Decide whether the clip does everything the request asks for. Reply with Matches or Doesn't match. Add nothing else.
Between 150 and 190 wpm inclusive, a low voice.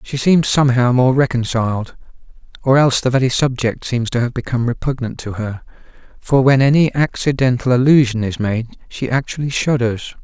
Matches